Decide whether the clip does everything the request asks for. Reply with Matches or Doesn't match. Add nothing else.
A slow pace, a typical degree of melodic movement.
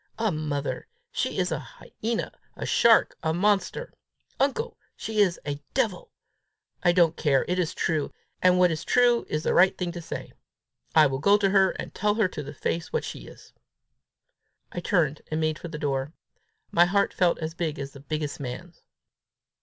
Doesn't match